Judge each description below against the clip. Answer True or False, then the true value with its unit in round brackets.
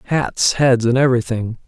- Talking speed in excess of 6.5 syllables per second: False (5.0 syllables/s)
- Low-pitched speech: True (125 Hz)